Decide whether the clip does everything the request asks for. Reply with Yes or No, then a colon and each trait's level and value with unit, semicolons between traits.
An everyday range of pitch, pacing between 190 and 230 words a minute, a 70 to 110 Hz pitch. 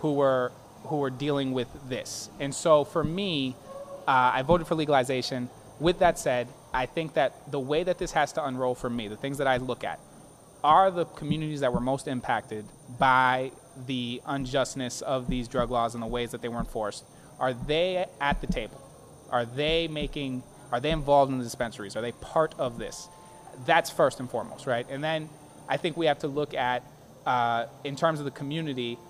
No: average, 3.8 semitones; average, 200 wpm; low, 135 Hz